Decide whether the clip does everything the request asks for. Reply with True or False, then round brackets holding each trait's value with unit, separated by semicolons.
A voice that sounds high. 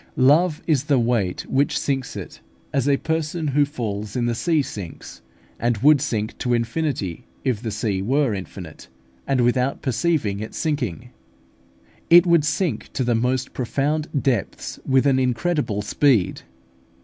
False (130 Hz)